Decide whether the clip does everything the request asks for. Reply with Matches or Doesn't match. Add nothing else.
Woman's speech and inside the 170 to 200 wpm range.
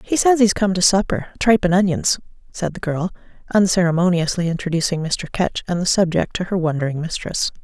Matches